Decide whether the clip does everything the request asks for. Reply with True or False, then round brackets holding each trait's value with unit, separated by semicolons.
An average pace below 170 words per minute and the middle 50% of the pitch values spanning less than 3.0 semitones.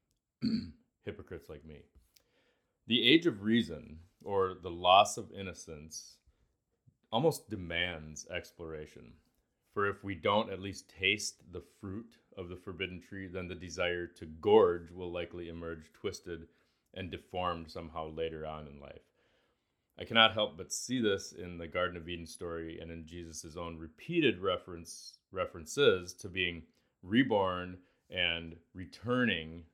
True (135 wpm; 2.5 semitones)